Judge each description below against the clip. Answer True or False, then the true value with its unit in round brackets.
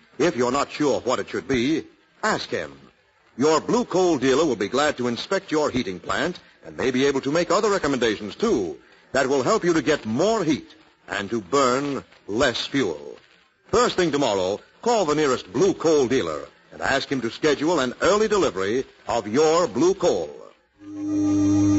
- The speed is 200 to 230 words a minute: False (180 wpm)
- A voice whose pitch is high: True (210 Hz)